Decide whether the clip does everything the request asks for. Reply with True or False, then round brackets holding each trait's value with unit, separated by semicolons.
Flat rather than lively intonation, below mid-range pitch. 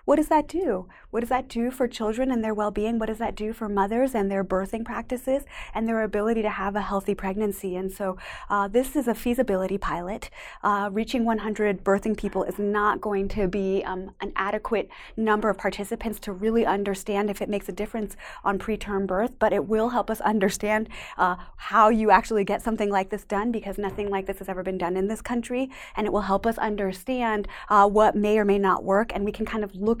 False (2.3 semitones; 210 Hz)